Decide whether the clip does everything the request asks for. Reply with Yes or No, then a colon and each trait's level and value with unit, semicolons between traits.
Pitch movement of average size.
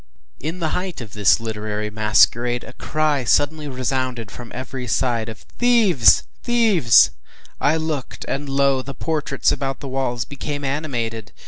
Yes: average, 4.5 semitones